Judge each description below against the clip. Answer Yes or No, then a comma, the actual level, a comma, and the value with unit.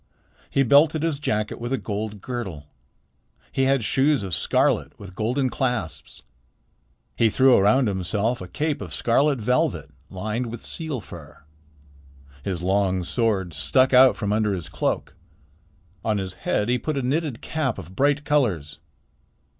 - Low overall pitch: Yes, low, 115 Hz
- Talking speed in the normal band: Yes, average, 150 wpm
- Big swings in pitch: Yes, wide, 5.7 semitones